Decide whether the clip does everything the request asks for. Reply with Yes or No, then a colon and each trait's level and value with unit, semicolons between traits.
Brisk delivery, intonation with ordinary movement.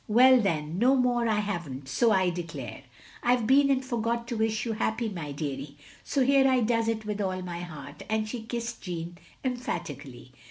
No: fast, 210 wpm; wide, 5.8 semitones